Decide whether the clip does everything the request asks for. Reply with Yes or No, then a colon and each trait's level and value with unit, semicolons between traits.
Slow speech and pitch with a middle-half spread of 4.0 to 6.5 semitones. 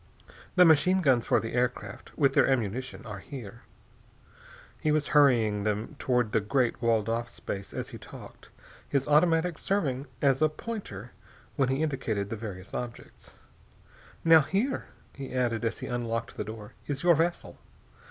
No: average, 160 wpm; average, 5.0 semitones